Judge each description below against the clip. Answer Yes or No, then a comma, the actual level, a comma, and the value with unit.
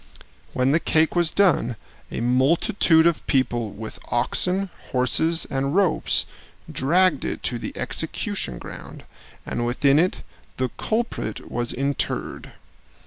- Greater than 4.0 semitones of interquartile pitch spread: Yes, wide, 5.6 semitones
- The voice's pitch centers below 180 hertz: Yes, medium, 140 Hz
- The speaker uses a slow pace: Yes, slow, 125 wpm